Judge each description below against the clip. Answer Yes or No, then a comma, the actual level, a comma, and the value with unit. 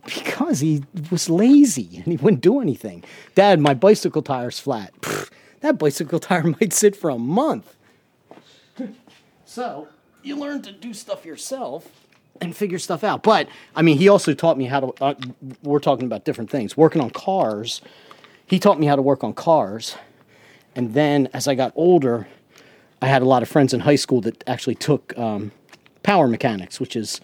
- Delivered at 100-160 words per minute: No, average, 185 wpm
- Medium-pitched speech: Yes, medium, 155 Hz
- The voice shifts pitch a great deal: Yes, wide, 6.9 semitones